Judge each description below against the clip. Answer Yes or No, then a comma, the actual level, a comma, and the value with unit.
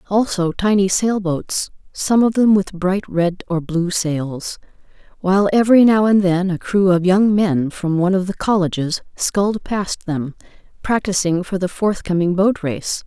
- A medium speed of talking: Yes, average, 165 wpm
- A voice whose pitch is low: No, high, 190 Hz